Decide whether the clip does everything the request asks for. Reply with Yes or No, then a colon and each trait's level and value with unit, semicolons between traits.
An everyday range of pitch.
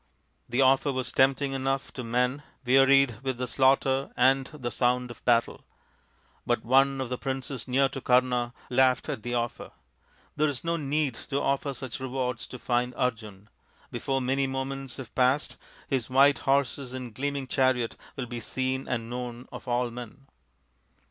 No: narrow, 1.7 semitones